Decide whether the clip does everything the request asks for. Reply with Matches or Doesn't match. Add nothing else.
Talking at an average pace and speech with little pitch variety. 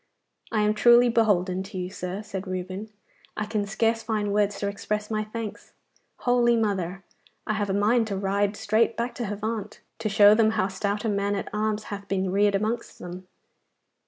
Matches